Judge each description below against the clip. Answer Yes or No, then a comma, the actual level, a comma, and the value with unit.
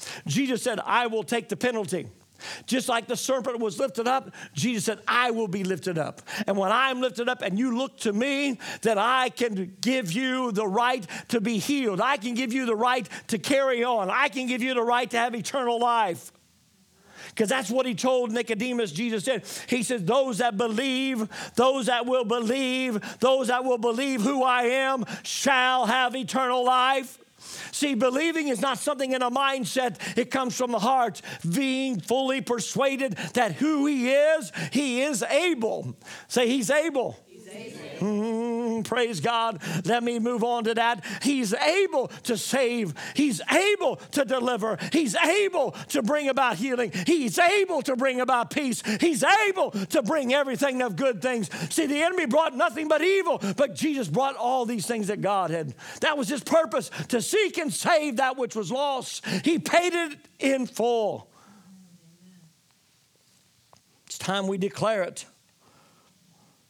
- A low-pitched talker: No, very high, 250 Hz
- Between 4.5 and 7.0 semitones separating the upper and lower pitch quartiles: No, average, 3.1 semitones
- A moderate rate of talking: Yes, average, 170 wpm